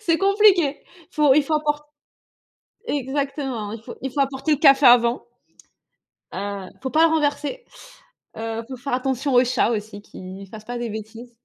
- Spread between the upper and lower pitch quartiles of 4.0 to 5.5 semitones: Yes, average, 4.5 semitones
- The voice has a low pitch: No, very high, 265 Hz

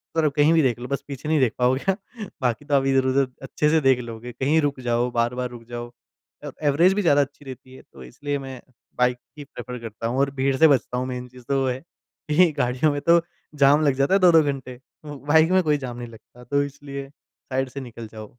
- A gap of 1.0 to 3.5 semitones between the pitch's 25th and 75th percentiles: Yes, average, 2.7 semitones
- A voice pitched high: No, low, 135 Hz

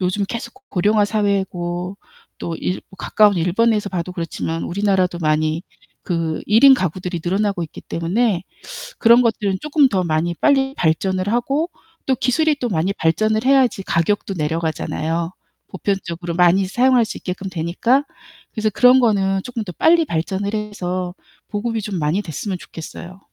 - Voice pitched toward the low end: No, high, 195 Hz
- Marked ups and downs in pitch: No, average, 4.3 semitones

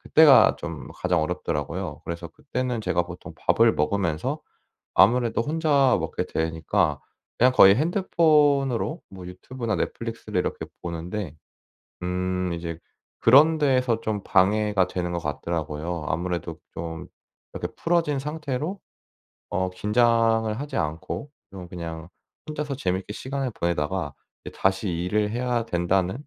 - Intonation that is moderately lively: No, wide, 6.8 semitones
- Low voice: Yes, very low, 95 Hz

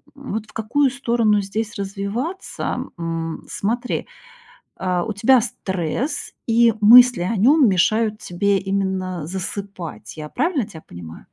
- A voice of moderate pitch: No, high, 205 Hz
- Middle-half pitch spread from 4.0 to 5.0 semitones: Yes, average, 4.4 semitones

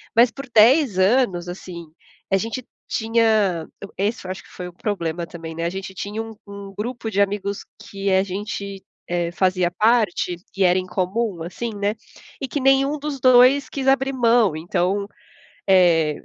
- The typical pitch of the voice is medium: No, high, 200 Hz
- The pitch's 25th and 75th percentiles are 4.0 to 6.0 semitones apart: Yes, average, 4.5 semitones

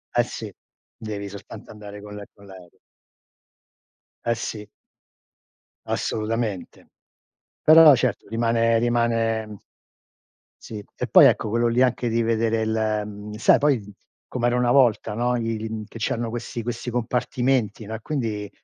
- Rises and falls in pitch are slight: Yes, narrow, 2.0 semitones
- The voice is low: Yes, low, 115 Hz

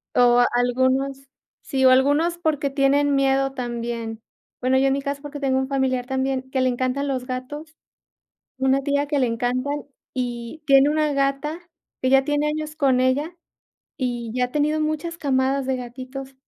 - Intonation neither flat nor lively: No, narrow, 2.0 semitones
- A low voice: No, very high, 270 Hz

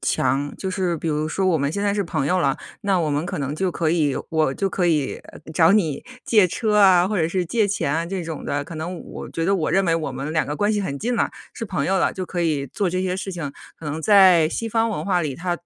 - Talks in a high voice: No, medium, 175 Hz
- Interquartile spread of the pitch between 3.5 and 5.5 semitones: Yes, average, 3.8 semitones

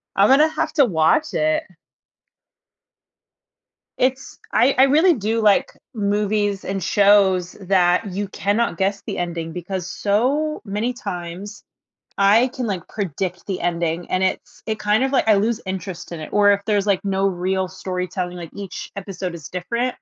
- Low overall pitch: No, high, 200 Hz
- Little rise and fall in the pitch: No, average, 3.5 semitones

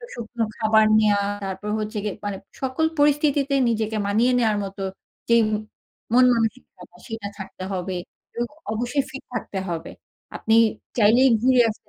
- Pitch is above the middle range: Yes, high, 225 Hz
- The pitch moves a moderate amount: Yes, average, 3.4 semitones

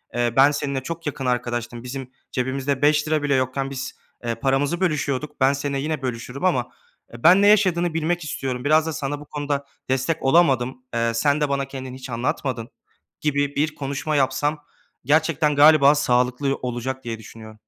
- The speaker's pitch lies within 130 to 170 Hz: Yes, medium, 140 Hz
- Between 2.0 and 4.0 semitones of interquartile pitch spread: Yes, average, 2.9 semitones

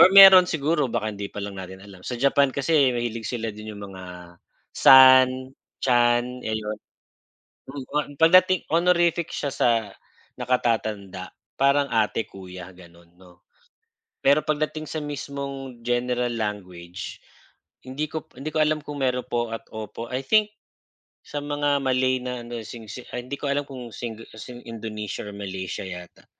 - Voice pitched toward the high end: No, low, 125 Hz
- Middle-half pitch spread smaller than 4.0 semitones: No, average, 5.2 semitones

